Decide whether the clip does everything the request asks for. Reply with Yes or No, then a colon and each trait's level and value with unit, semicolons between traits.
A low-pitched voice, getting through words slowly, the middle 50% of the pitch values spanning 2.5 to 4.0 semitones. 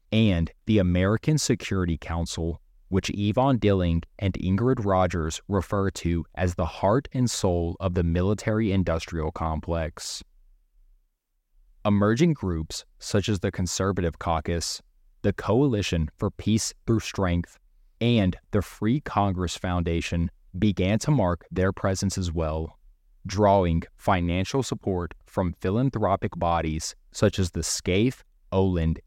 Yes: very low, 95 Hz; slow, 120 wpm; average, 3.7 semitones